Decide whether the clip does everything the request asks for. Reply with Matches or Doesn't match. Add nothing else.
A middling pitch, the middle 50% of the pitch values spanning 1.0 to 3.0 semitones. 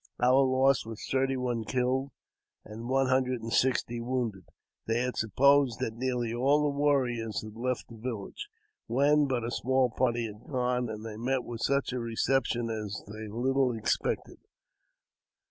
Doesn't match